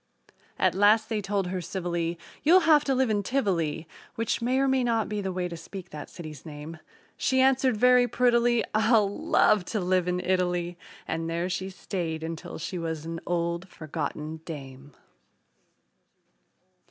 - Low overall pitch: No, medium, 185 Hz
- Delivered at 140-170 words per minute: Yes, average, 165 wpm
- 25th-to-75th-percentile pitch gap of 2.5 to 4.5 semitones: No, wide, 5.4 semitones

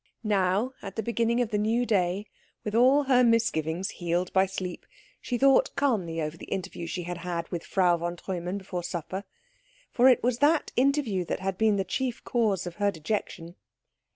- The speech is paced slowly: No, average, 185 wpm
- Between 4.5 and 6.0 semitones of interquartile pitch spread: Yes, average, 4.9 semitones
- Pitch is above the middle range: Yes, high, 195 Hz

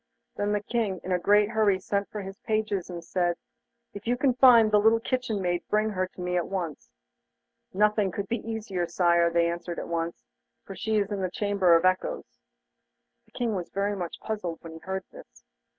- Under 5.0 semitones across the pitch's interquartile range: Yes, average, 3.3 semitones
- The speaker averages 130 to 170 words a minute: No, average, 200 wpm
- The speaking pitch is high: Yes, high, 195 Hz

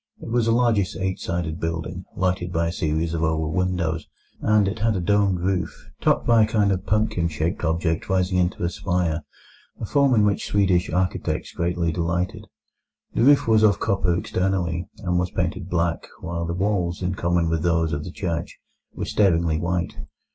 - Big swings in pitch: No, narrow, 2.6 semitones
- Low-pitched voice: Yes, very low, 90 Hz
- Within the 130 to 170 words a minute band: No, average, 185 wpm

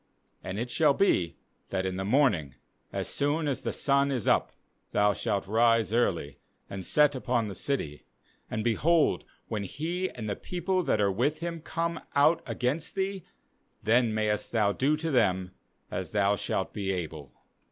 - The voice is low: Yes, low, 115 Hz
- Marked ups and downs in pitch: Yes, wide, 7.0 semitones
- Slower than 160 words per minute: No, average, 170 wpm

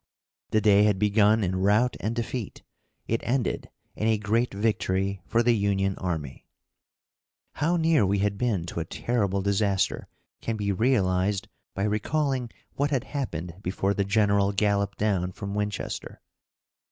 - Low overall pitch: Yes, low, 105 Hz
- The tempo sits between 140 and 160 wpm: Yes, average, 150 wpm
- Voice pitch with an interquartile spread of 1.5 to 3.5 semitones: Yes, average, 2.8 semitones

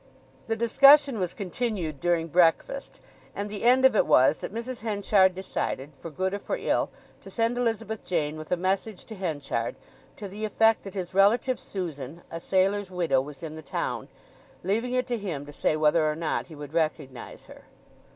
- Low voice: No, high, 190 Hz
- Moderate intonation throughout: No, wide, 5.9 semitones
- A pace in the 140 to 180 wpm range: No, average, 190 wpm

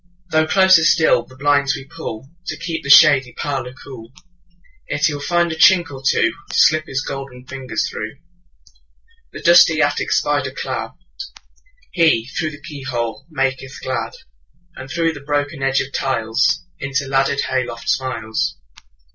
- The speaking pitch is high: No, medium, 140 Hz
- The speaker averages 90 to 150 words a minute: Yes, average, 140 wpm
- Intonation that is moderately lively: Yes, average, 4.0 semitones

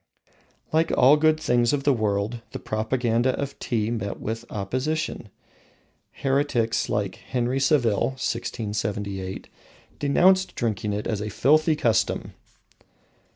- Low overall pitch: Yes, low, 120 Hz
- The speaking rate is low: Yes, slow, 115 wpm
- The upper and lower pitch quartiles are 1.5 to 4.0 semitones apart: No, average, 4.8 semitones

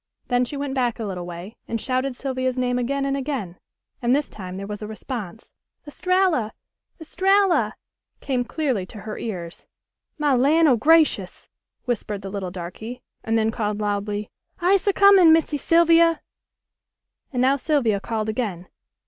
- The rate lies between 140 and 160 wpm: Yes, average, 155 wpm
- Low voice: No, high, 245 Hz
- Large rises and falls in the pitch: Yes, wide, 5.8 semitones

